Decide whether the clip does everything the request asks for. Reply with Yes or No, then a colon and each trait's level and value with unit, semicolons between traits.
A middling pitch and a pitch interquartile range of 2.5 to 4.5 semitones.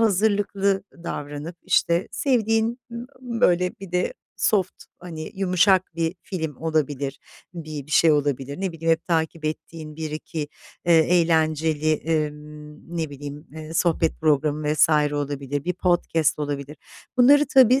Yes: medium, 160 Hz; average, 3.3 semitones